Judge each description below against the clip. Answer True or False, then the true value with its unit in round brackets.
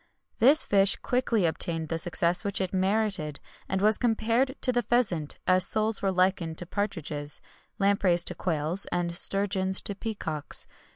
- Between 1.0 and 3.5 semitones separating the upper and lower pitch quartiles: False (4.0 semitones)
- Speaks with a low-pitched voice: False (190 Hz)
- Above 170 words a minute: False (155 wpm)